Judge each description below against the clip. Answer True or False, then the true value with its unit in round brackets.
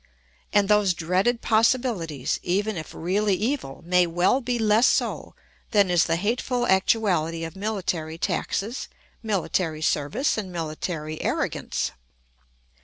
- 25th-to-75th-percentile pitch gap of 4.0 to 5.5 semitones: True (4.7 semitones)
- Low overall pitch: False (190 Hz)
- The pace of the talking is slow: True (120 wpm)